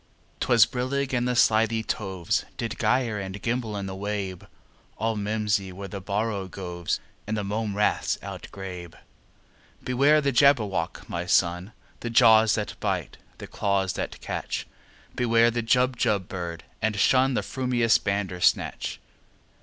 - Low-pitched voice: Yes, low, 105 Hz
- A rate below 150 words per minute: Yes, average, 140 wpm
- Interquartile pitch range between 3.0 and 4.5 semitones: Yes, average, 3.6 semitones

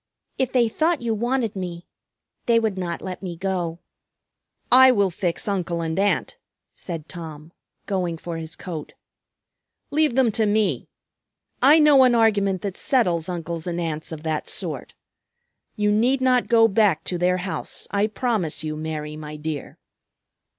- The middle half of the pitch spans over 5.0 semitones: Yes, wide, 5.6 semitones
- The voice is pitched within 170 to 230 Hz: Yes, high, 190 Hz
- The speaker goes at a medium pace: Yes, average, 155 wpm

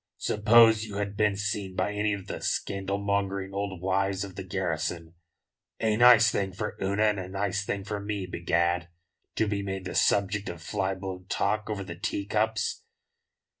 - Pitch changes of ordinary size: No, narrow, 1.7 semitones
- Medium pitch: No, low, 100 Hz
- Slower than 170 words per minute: No, average, 175 wpm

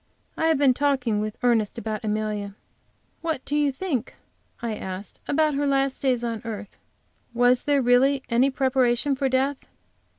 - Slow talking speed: No, average, 160 wpm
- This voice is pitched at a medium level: No, very high, 255 Hz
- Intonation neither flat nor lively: Yes, average, 3.7 semitones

